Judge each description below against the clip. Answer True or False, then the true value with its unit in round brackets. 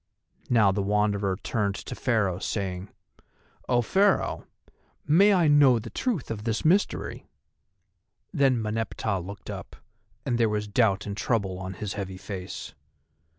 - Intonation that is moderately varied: True (4.0 semitones)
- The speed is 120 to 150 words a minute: True (140 wpm)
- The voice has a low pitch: True (105 Hz)